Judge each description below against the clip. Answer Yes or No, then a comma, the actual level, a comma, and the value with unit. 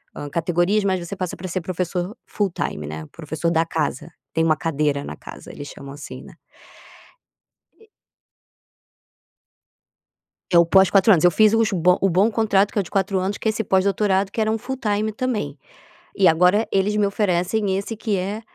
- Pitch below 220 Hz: Yes, high, 190 Hz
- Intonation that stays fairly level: No, average, 3.8 semitones